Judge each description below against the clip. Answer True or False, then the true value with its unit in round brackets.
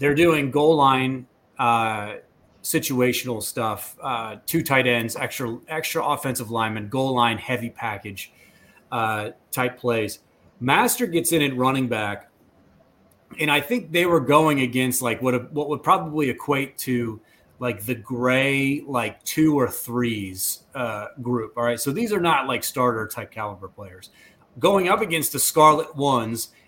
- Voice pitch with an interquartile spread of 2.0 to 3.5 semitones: False (4.0 semitones)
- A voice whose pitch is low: True (125 Hz)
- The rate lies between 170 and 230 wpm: False (155 wpm)